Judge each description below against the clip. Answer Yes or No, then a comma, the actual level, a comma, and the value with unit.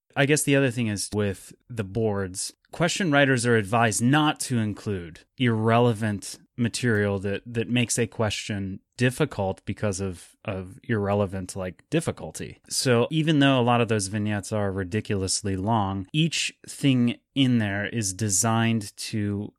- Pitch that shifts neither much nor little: Yes, average, 3.5 semitones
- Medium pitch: No, low, 110 Hz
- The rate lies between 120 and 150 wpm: Yes, average, 145 wpm